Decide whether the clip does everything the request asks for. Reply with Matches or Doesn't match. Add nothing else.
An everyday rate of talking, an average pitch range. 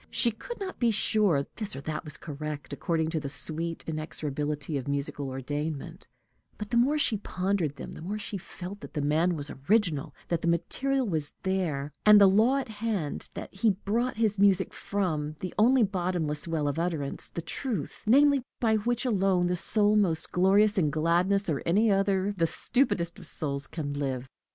Doesn't match